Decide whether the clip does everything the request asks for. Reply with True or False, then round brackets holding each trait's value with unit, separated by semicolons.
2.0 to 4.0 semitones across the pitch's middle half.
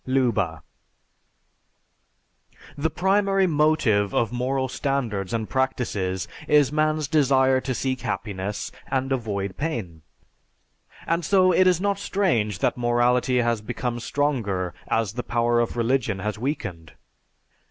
False (5.5 semitones)